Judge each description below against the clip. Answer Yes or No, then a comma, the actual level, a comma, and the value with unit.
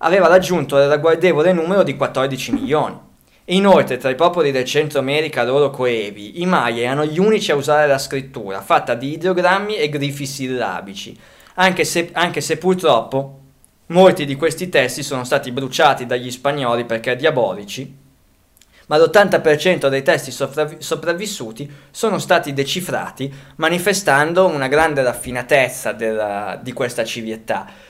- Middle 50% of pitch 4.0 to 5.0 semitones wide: Yes, average, 4.6 semitones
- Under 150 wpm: Yes, average, 140 wpm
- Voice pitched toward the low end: No, medium, 145 Hz